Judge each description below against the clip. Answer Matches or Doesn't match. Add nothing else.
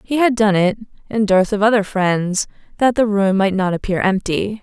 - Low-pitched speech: Doesn't match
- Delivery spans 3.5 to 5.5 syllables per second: Matches